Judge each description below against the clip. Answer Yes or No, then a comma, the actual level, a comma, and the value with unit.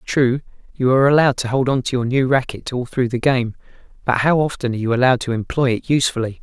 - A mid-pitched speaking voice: No, low, 125 Hz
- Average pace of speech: No, fast, 235 wpm